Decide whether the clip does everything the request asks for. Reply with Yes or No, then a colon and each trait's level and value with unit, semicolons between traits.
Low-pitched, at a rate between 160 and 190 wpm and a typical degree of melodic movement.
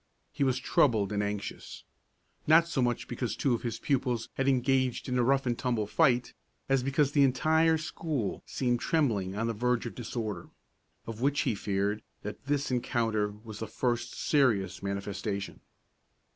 Yes: low, 120 Hz; average, 165 wpm; average, 4.1 semitones